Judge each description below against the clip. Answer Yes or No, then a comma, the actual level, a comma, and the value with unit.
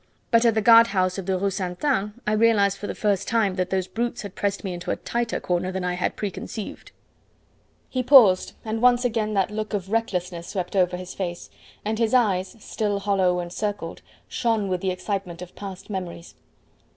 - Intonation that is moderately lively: Yes, average, 3.1 semitones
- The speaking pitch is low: No, high, 200 Hz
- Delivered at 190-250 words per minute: Yes, fast, 205 wpm